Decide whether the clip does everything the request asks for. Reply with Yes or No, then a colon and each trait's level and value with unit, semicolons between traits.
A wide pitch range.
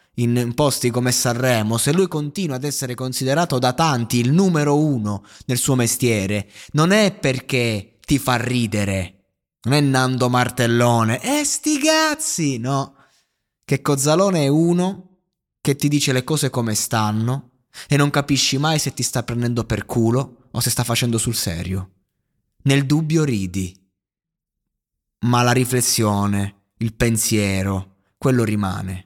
No: average, 4.2 semitones